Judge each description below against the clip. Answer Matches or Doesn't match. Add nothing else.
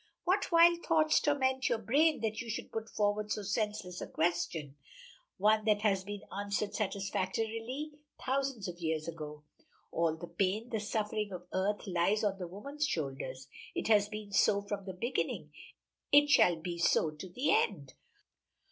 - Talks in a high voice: Matches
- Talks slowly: Doesn't match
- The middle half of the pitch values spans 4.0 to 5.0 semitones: Matches